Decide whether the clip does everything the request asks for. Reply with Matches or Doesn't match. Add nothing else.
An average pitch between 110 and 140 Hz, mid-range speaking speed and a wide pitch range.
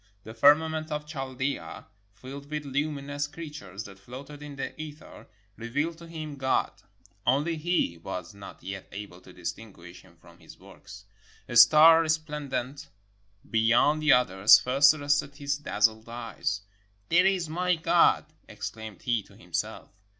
Matches